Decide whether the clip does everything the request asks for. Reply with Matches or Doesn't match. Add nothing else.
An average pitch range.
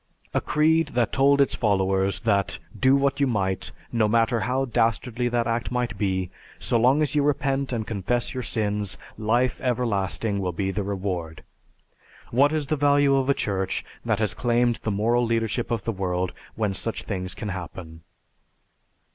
Matches